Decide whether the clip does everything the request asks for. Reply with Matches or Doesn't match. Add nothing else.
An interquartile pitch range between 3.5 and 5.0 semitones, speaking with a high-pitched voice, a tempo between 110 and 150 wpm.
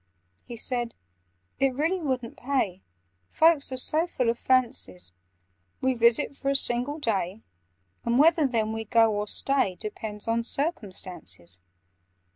Matches